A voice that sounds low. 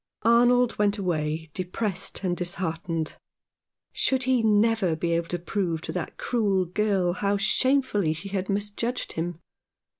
No: high, 195 Hz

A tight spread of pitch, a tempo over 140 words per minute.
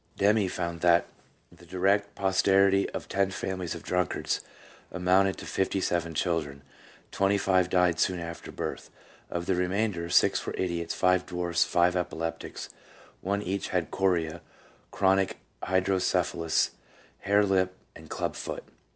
No: narrow, 2.0 semitones; slow, 135 wpm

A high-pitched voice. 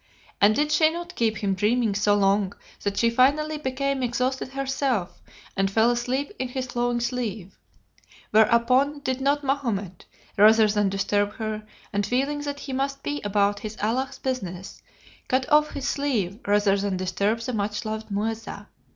Yes: high, 235 Hz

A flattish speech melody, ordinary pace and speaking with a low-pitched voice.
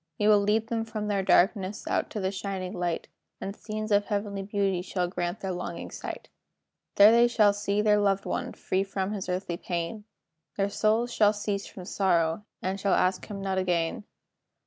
No: narrow, 2.0 semitones; average, 190 wpm; high, 200 Hz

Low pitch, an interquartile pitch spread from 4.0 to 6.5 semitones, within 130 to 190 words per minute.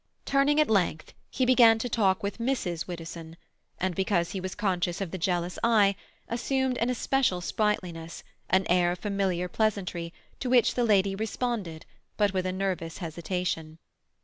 No: high, 190 Hz; average, 4.3 semitones; average, 160 wpm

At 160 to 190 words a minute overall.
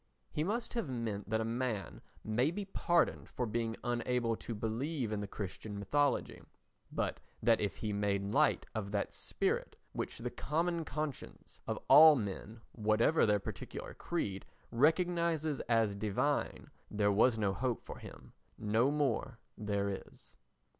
No: average, 150 wpm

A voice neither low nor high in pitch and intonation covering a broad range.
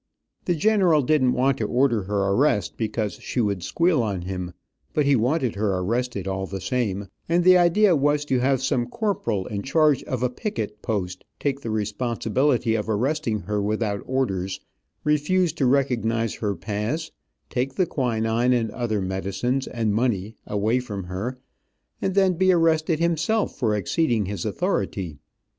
No: low, 120 Hz; wide, 6.1 semitones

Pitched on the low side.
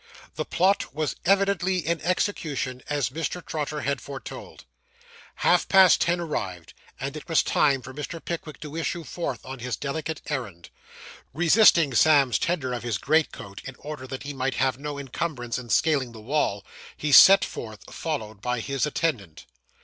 No: medium, 145 Hz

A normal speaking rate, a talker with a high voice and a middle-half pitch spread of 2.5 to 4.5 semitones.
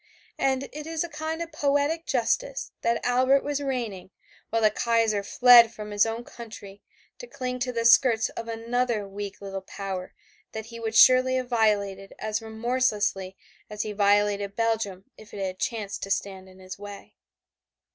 Yes: average, 170 wpm; high, 225 Hz; average, 3.8 semitones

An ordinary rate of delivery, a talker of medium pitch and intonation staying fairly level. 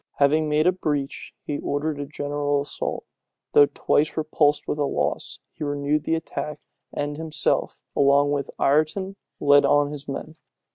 Yes: average, 150 wpm; medium, 145 Hz; narrow, 1.3 semitones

